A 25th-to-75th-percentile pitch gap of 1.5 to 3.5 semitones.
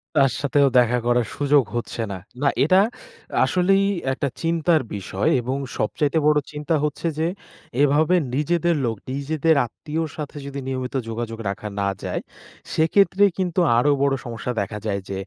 No: average, 4.9 semitones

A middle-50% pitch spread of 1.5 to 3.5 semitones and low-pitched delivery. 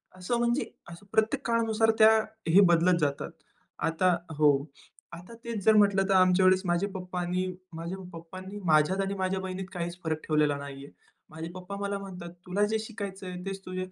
No: average, 2.8 semitones; medium, 185 Hz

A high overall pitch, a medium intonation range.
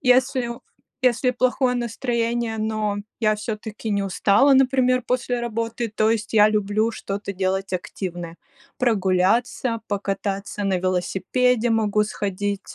Yes: high, 215 Hz; average, 3.4 semitones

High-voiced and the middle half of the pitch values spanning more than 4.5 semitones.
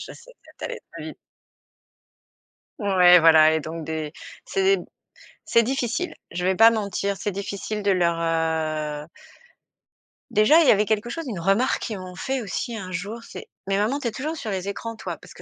Yes: high, 200 Hz; average, 5.0 semitones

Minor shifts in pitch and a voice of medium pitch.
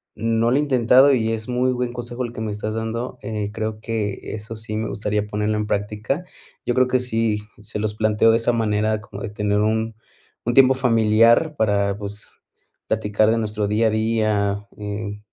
No: narrow, 1.8 semitones; low, 110 Hz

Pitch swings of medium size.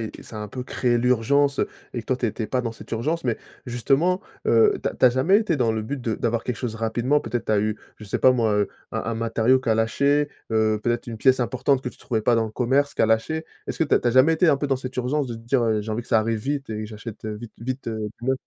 Yes: average, 3.2 semitones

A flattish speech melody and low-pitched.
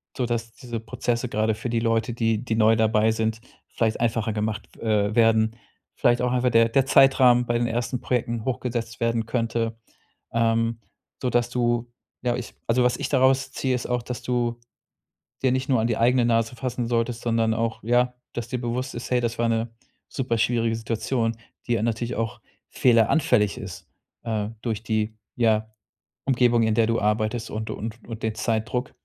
Yes: narrow, 1.5 semitones; low, 115 Hz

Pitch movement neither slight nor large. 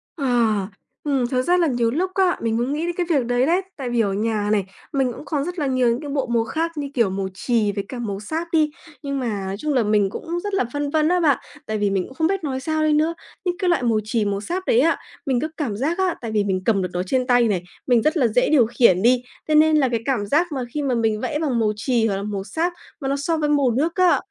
No: wide, 5.7 semitones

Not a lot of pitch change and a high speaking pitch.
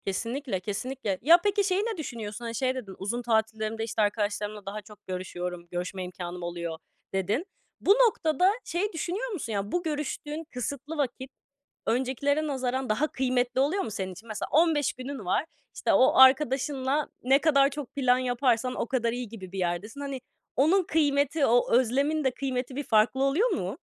No: average, 5.2 semitones; very high, 255 Hz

